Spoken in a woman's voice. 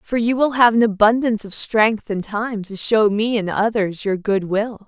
Yes: female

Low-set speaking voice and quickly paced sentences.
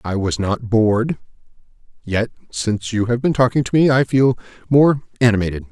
No: low, 115 Hz; average, 170 wpm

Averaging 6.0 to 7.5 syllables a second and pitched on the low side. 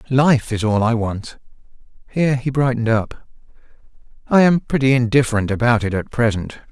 No: 5.6 syllables/s; low, 120 Hz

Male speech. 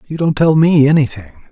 Yes: male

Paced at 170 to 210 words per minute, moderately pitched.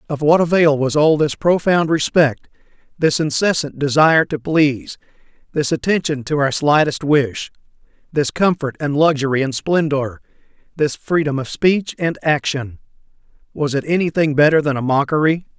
No: average, 145 wpm; medium, 150 Hz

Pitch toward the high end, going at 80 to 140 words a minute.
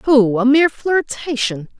Yes: very high, 260 Hz; slow, 135 wpm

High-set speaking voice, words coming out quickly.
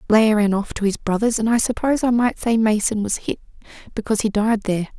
Yes: high, 215 Hz; fast, 230 wpm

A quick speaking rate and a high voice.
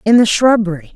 No: average, 190 wpm; high, 205 Hz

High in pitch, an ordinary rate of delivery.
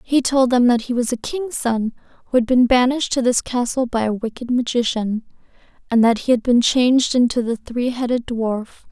No: high, 245 Hz; fast, 210 wpm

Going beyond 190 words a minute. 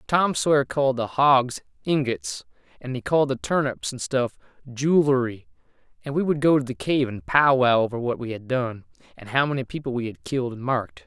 Yes: average, 200 wpm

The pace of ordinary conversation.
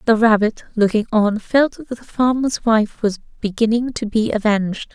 Yes: average, 170 wpm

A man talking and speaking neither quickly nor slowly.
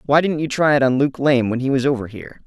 No: male; fast, 315 wpm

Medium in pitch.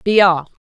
Yes: medium, 180 Hz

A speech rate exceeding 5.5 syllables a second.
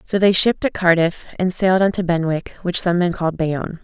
Yes: 5.7 syllables/s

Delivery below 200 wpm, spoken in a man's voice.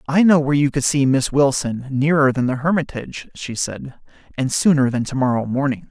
No: fast, 205 wpm; male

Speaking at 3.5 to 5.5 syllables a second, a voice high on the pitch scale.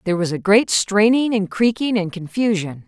Yes: 5.1 syllables/s; high, 205 Hz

